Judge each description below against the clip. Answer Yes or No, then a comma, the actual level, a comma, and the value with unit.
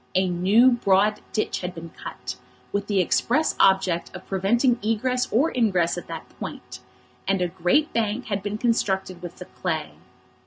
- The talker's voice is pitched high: Yes, high, 195 Hz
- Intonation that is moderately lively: Yes, average, 4.1 semitones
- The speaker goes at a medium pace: Yes, average, 165 wpm